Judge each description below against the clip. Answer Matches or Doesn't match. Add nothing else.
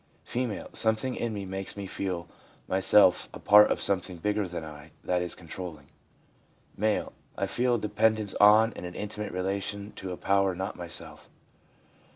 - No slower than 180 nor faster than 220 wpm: Matches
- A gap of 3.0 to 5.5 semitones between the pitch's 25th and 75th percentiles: Doesn't match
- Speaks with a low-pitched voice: Matches